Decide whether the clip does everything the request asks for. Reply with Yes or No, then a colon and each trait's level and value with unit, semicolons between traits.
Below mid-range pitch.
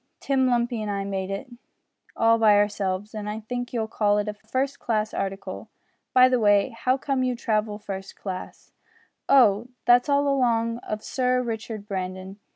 No: high, 220 Hz